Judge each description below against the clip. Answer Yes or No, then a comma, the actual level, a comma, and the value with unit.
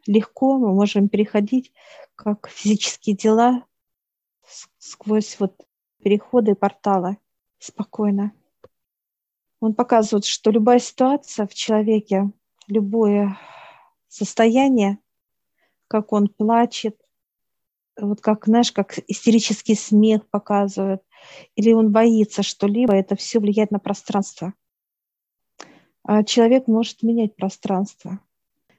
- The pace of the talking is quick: No, slow, 95 wpm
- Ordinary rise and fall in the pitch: No, narrow, 2.1 semitones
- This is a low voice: No, high, 215 Hz